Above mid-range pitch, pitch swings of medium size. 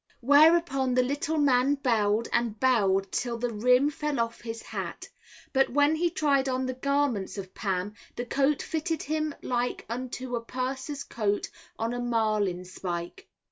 Yes: very high, 250 Hz; average, 4.0 semitones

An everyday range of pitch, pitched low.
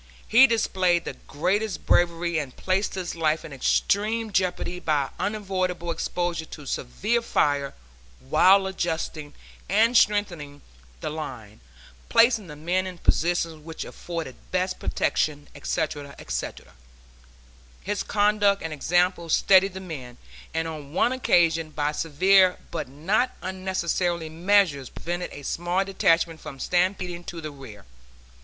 No: average, 3.7 semitones; medium, 175 Hz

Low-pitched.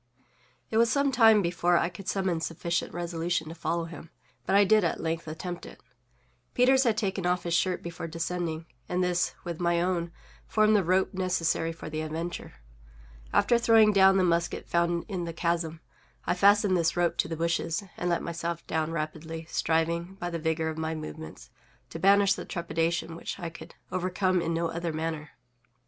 No: medium, 170 Hz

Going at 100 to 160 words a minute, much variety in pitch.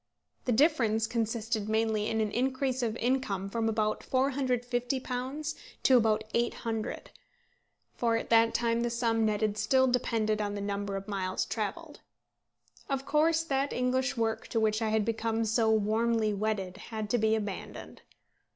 No: average, 150 wpm; narrow, 2.6 semitones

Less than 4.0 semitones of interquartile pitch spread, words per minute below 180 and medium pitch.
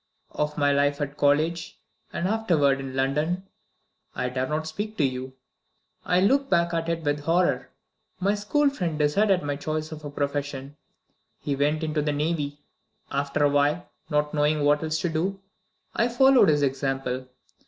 Yes: average, 3.1 semitones; average, 165 wpm; medium, 150 Hz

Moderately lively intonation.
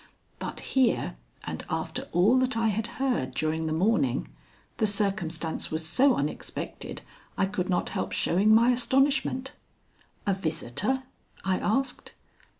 No: wide, 7.4 semitones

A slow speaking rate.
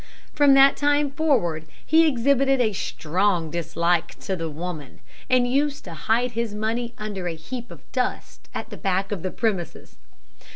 No: average, 165 wpm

